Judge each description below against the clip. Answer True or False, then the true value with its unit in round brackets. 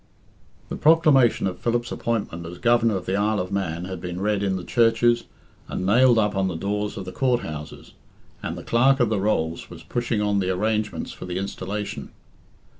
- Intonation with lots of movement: False (4.0 semitones)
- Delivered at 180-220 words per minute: True (195 wpm)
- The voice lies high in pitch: False (105 Hz)